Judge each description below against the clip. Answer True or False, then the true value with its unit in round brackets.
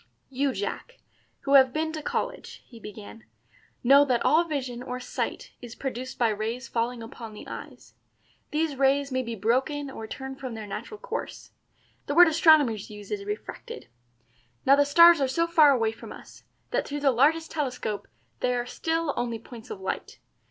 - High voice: True (265 Hz)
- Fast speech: False (180 wpm)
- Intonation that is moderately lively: True (4.5 semitones)